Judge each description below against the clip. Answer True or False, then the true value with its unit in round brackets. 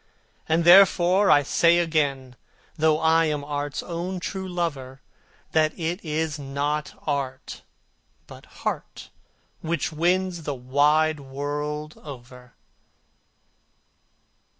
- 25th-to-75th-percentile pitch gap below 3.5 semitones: True (2.9 semitones)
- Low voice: False (155 Hz)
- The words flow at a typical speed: False (105 wpm)